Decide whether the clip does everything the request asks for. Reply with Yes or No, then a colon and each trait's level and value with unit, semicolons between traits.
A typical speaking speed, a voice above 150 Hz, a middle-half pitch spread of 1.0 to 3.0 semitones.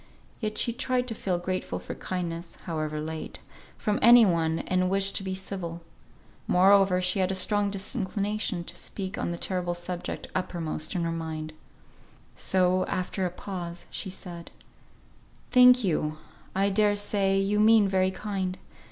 Yes: average, 155 wpm; medium, 185 Hz; average, 2.7 semitones